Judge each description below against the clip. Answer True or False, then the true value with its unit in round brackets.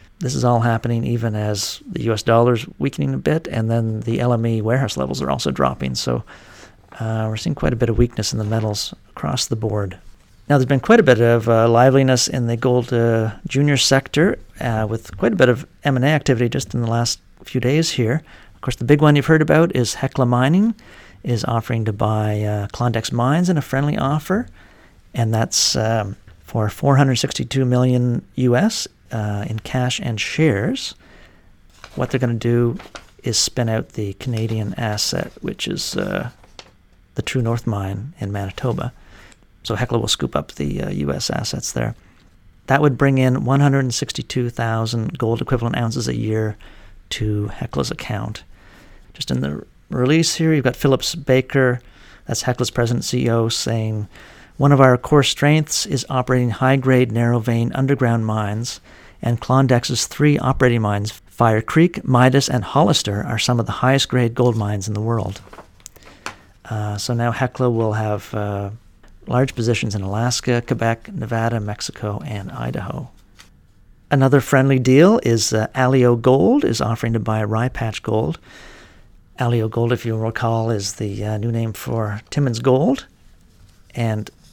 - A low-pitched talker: True (115 Hz)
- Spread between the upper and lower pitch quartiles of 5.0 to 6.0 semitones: False (3.3 semitones)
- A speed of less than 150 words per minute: False (165 wpm)